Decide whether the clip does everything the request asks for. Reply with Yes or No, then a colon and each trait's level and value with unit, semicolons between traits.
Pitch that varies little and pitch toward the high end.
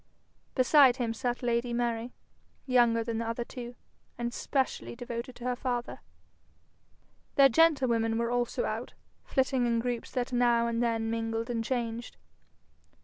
Yes: narrow, 1.3 semitones; high, 240 Hz